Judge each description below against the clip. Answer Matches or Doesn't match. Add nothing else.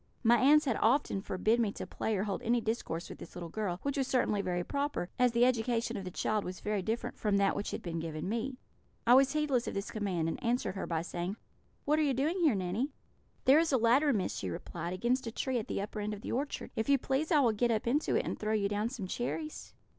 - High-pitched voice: Matches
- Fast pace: Matches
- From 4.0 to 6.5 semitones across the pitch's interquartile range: Matches